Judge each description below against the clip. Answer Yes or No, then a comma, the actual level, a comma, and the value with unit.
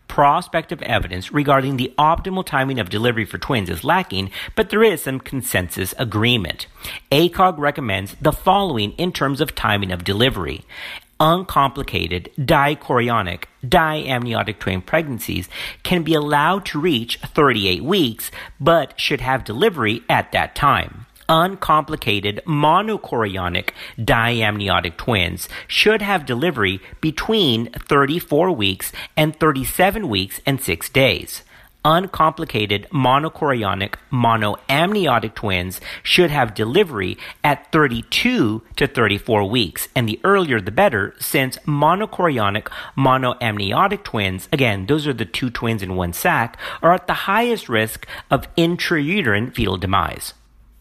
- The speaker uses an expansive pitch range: Yes, wide, 7.1 semitones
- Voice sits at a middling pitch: No, low, 130 Hz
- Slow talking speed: Yes, slow, 120 wpm